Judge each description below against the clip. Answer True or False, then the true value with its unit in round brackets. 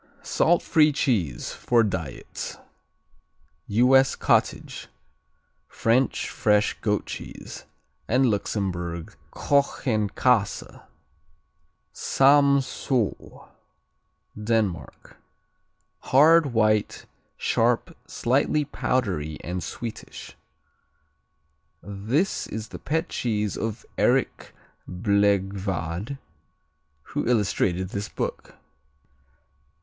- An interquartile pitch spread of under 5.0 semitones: False (5.3 semitones)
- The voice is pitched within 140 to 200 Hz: False (110 Hz)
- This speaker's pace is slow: True (70 wpm)